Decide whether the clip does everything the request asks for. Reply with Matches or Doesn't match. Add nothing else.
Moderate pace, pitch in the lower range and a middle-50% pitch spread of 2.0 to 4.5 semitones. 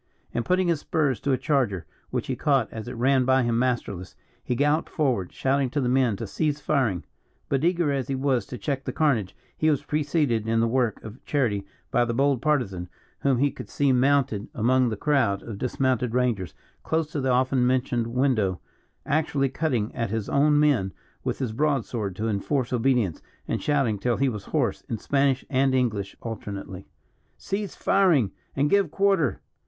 Matches